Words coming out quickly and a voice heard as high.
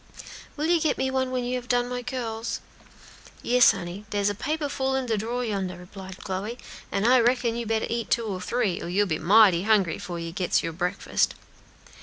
Yes: fast, 210 wpm; high, 225 Hz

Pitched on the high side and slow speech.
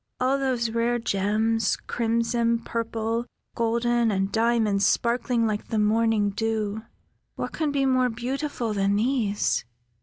Yes: high, 230 Hz; slow, 125 wpm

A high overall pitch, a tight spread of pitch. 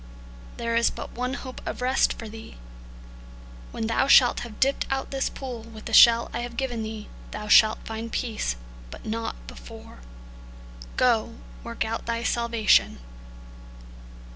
Yes: high, 230 Hz; narrow, 1.9 semitones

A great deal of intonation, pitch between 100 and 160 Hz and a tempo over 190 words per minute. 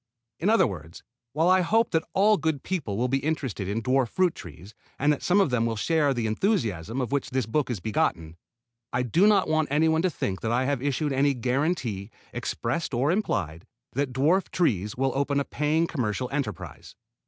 Yes: wide, 5.9 semitones; low, 135 Hz; average, 200 wpm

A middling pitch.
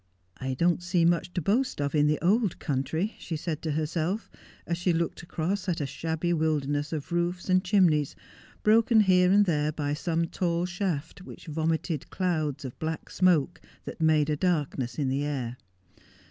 Yes: medium, 165 Hz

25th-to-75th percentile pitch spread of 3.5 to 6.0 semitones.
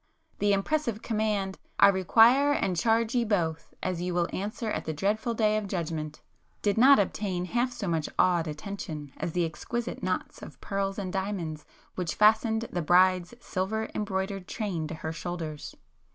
Yes: average, 3.9 semitones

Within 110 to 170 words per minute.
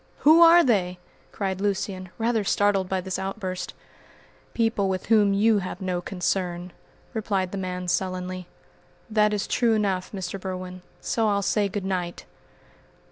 Yes: average, 145 wpm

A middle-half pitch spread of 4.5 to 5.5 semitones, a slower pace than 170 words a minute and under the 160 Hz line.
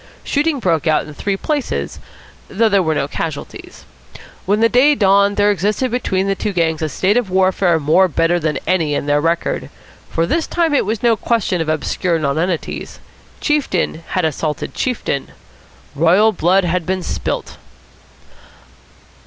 No: average, 4.9 semitones; average, 160 wpm; medium, 185 Hz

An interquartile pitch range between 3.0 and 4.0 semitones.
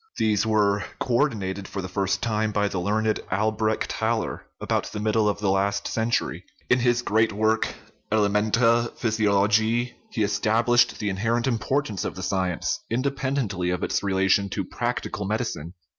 No: narrow, 2.4 semitones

